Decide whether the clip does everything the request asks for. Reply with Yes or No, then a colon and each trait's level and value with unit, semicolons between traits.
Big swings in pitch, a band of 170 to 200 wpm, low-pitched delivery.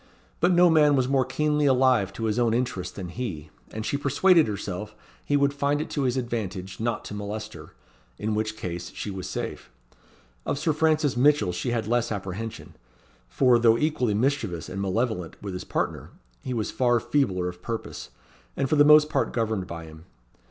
Yes: wide, 6.1 semitones; average, 190 wpm; low, 115 Hz